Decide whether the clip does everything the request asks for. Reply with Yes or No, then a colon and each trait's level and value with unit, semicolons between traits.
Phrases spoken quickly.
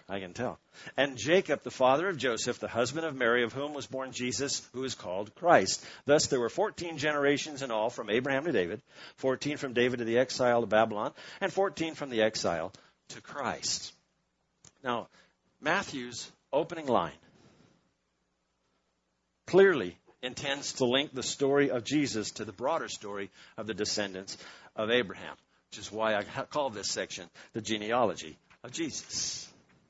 No: average, 160 wpm